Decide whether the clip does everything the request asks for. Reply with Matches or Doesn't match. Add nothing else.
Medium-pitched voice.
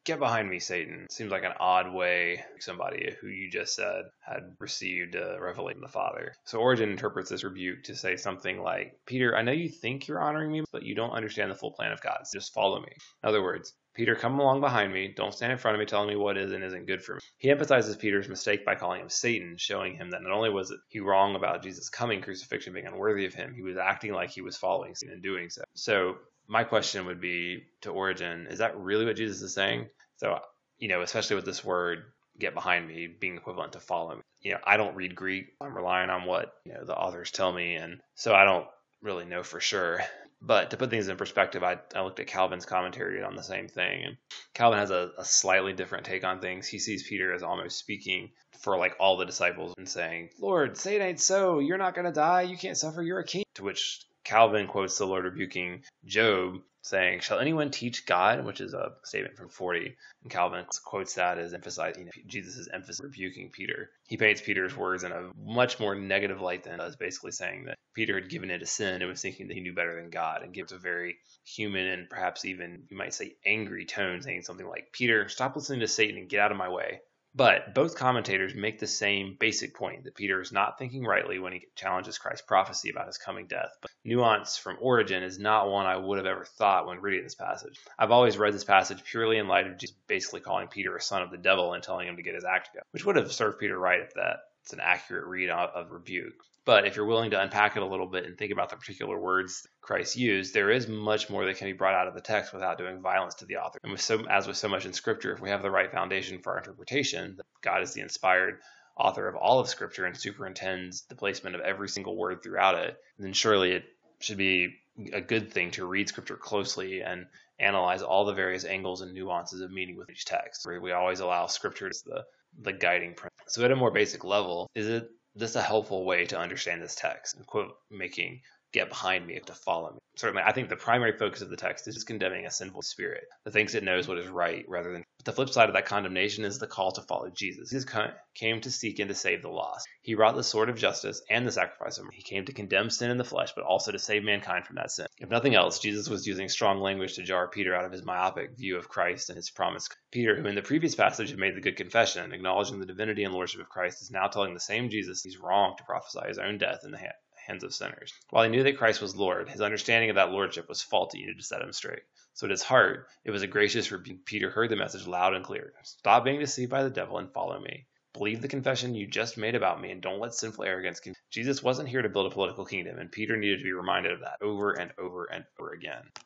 Doesn't match